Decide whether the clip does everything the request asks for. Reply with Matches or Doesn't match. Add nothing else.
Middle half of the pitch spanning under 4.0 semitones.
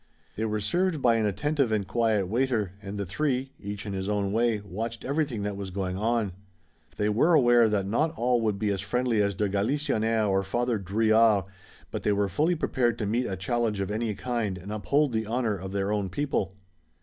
Matches